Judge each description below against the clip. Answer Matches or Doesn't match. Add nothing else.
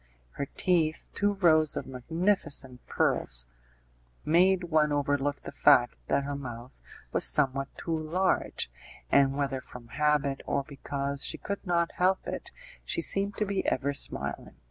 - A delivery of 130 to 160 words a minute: Matches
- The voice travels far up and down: Doesn't match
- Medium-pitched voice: Matches